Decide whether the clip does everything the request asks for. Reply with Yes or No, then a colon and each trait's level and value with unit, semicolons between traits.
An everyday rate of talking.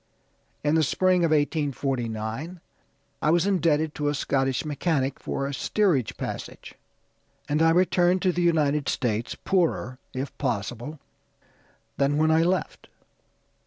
No: slow, 130 wpm